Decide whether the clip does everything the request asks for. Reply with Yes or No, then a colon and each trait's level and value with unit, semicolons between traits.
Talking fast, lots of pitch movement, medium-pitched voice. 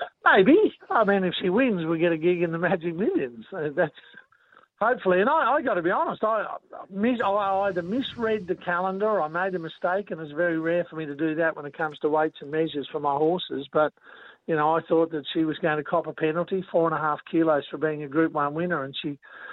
No: fast, 250 wpm; average, 3.5 semitones; medium, 170 Hz